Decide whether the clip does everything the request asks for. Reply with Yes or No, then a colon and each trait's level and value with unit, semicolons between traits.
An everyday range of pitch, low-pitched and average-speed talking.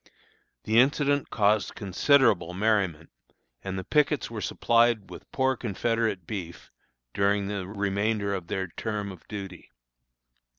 No: average, 3.2 semitones; low, 100 Hz; slow, 125 wpm